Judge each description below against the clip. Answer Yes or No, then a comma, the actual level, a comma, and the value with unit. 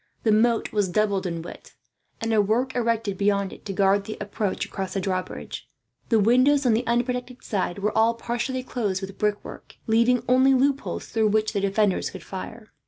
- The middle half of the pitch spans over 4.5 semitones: No, average, 3.2 semitones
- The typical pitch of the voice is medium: No, high, 215 Hz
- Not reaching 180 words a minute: No, average, 185 wpm